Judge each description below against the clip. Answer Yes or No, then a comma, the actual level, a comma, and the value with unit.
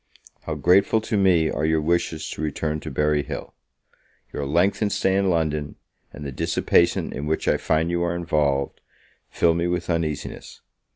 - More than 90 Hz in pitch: No, very low, 80 Hz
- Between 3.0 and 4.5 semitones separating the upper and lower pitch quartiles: No, narrow, 2.4 semitones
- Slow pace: No, average, 170 wpm